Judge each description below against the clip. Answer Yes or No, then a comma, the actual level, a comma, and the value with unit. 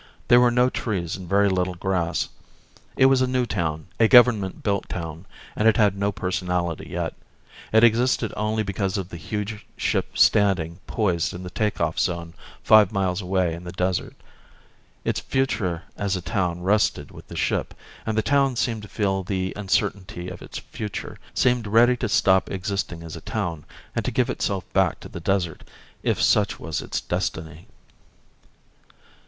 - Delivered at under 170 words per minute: No, average, 175 wpm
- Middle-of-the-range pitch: No, very low, 95 Hz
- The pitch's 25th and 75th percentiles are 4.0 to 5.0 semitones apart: No, average, 3.6 semitones